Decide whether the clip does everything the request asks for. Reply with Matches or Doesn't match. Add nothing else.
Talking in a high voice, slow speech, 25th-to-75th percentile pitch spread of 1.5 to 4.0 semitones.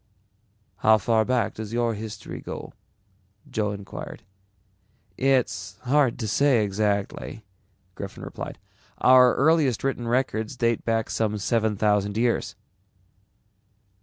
Doesn't match